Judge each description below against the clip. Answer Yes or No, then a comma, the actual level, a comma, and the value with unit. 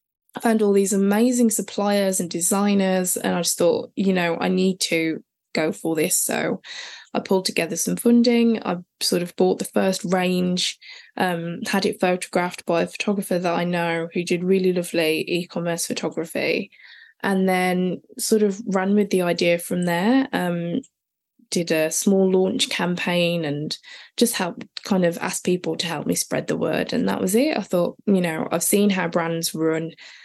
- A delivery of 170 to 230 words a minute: Yes, average, 180 wpm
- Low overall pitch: No, medium, 185 Hz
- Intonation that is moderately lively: Yes, average, 3.2 semitones